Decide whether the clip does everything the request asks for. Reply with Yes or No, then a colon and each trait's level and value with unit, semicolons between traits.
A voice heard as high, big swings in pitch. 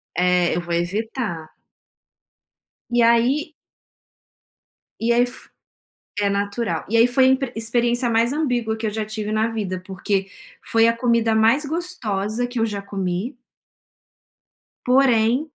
No: high, 225 Hz; average, 3.3 semitones